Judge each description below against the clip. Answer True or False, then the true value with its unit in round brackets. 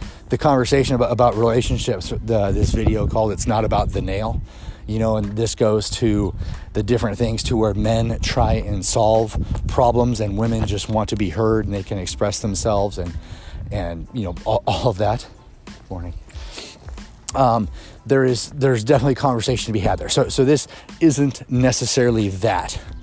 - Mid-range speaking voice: False (110 Hz)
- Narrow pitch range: False (3.3 semitones)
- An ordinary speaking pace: True (175 wpm)